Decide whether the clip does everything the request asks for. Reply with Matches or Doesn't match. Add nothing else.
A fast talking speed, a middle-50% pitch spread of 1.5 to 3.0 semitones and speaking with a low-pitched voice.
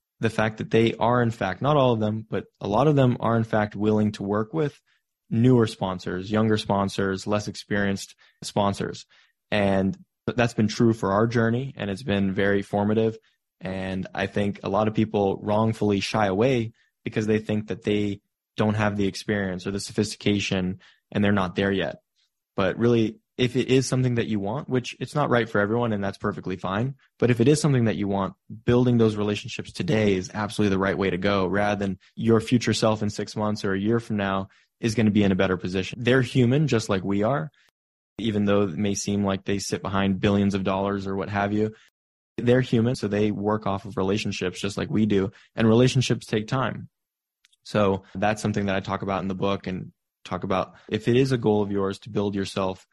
Matches